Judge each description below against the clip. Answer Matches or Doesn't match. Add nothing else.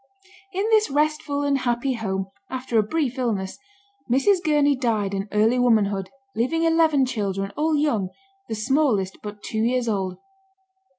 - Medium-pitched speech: Doesn't match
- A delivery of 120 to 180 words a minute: Matches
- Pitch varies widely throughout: Matches